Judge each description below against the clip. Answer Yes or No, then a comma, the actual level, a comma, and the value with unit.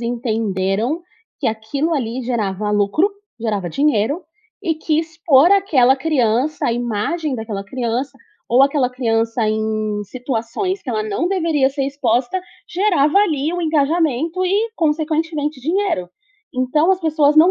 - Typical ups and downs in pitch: No, wide, 6.1 semitones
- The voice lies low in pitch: No, very high, 270 Hz